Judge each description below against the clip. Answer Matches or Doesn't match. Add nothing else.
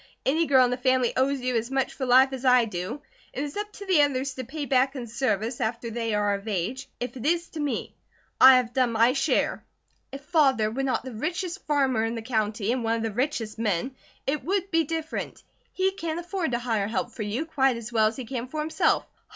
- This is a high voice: Matches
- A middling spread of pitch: Matches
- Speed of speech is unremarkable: Doesn't match